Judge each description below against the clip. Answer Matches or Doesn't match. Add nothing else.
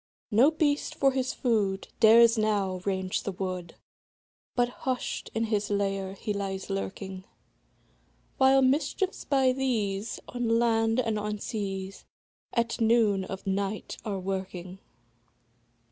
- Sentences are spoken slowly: Matches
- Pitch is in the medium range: Doesn't match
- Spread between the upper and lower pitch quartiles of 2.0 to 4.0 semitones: Matches